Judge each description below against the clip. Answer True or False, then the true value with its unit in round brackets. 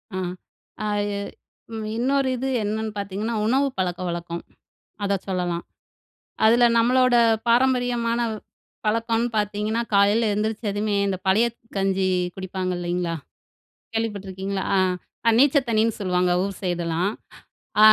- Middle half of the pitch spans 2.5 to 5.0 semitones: True (3.5 semitones)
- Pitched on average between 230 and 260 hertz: False (205 Hz)